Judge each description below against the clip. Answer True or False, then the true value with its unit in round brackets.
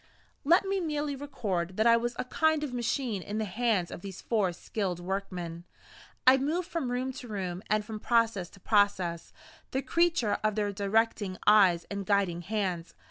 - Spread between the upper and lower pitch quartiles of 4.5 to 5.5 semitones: True (5.0 semitones)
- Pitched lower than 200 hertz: False (215 Hz)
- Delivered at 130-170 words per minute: False (180 wpm)